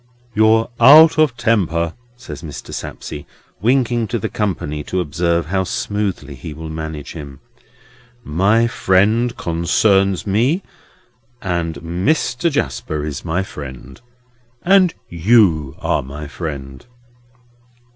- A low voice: Yes, very low, 90 Hz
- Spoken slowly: Yes, slow, 115 wpm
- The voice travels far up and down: Yes, wide, 6.6 semitones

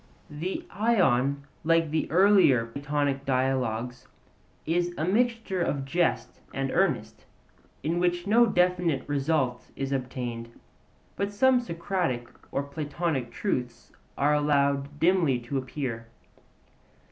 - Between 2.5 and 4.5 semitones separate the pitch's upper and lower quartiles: No, average, 5.3 semitones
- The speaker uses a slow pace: Yes, slow, 115 wpm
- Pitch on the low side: No, medium, 145 Hz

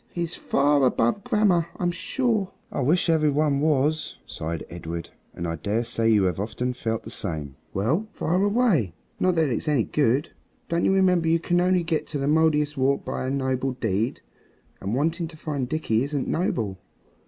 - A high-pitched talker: No, medium, 145 Hz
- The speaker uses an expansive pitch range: Yes, wide, 6.6 semitones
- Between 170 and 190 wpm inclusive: Yes, average, 180 wpm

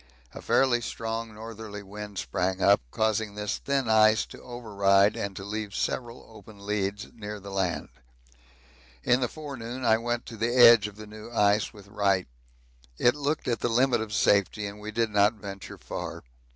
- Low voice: Yes, low, 110 Hz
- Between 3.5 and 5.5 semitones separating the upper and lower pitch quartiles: No, narrow, 2.5 semitones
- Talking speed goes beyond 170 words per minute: Yes, average, 180 wpm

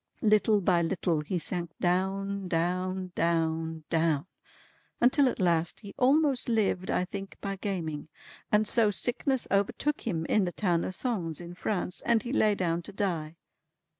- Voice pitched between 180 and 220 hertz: Yes, medium, 185 Hz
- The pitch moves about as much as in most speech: Yes, average, 3.9 semitones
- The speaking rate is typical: Yes, average, 160 wpm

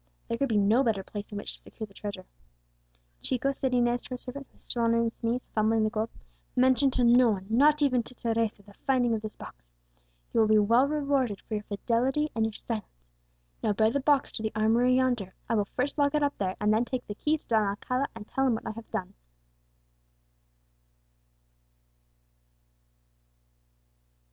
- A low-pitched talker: No, high, 230 Hz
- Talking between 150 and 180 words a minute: No, average, 200 wpm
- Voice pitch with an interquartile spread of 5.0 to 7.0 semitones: No, average, 3.2 semitones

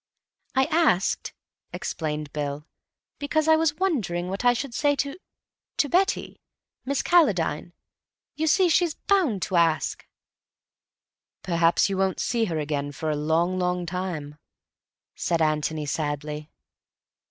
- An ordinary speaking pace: No, slow, 125 wpm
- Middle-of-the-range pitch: Yes, medium, 180 Hz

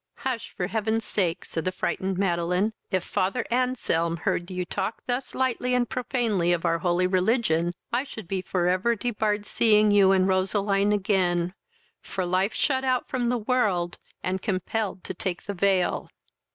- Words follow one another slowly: No, average, 165 wpm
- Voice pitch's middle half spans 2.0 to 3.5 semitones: No, average, 3.9 semitones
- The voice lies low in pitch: No, high, 195 Hz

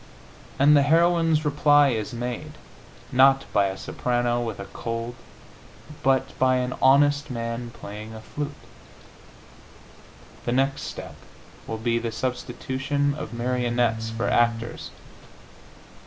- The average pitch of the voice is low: Yes, low, 125 Hz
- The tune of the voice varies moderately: Yes, average, 3.1 semitones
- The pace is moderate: No, slow, 120 wpm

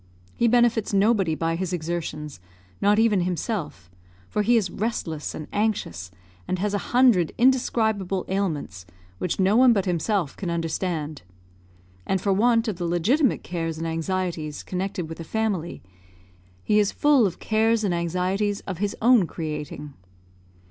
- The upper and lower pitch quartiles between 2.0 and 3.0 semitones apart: No, average, 4.7 semitones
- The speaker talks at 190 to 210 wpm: No, average, 150 wpm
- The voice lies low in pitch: No, high, 190 Hz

